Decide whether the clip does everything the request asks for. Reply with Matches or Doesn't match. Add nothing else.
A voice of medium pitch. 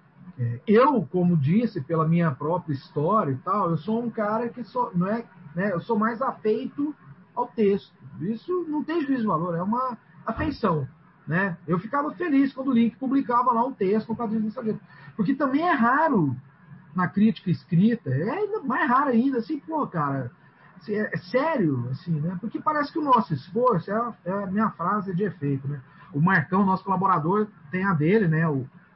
Doesn't match